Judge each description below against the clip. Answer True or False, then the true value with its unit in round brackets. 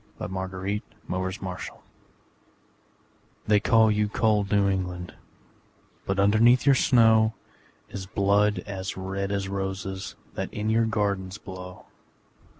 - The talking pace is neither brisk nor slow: False (125 wpm)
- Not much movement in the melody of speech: True (2.1 semitones)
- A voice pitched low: True (100 Hz)